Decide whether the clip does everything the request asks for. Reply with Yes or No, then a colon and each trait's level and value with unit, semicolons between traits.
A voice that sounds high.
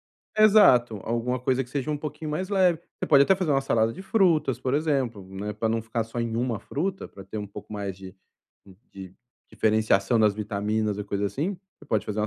No: low, 115 Hz